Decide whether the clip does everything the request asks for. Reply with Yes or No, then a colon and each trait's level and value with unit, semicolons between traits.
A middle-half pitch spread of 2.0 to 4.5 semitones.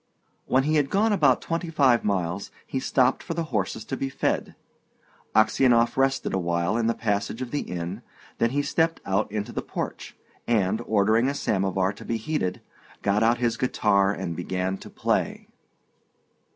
No: wide, 5.4 semitones